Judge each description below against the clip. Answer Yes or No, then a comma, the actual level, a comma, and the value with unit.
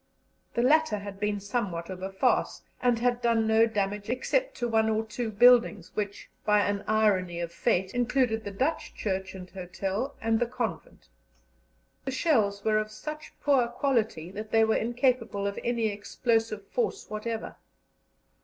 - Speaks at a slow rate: No, average, 165 wpm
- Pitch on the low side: No, high, 220 Hz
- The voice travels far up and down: No, average, 3.2 semitones